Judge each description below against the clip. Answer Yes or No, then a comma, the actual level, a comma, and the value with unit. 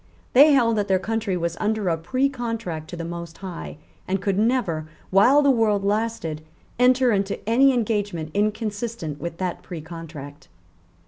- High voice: Yes, high, 200 Hz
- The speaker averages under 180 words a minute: Yes, average, 150 wpm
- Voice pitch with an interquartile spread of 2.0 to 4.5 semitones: No, average, 5.2 semitones